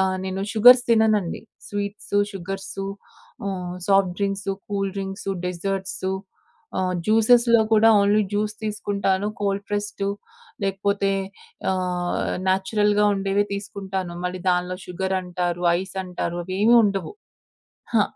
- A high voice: Yes, high, 195 Hz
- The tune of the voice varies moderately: No, narrow, 1.6 semitones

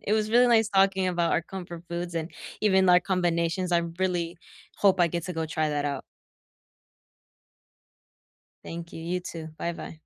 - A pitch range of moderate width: No, narrow, 2.2 semitones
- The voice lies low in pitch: No, medium, 175 Hz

